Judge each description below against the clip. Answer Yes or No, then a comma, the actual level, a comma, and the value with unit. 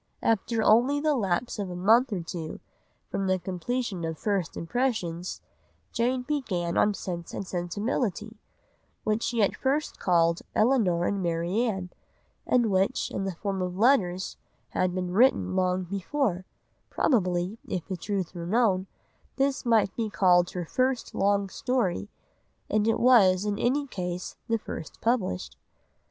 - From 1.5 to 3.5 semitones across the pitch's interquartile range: No, average, 4.7 semitones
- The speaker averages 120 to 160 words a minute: Yes, average, 145 wpm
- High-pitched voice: Yes, high, 195 Hz